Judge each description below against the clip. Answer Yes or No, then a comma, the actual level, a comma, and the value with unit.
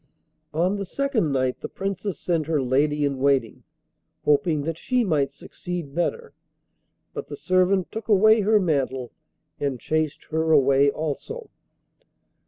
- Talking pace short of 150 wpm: Yes, average, 140 wpm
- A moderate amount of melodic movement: No, wide, 5.8 semitones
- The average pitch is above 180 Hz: No, medium, 160 Hz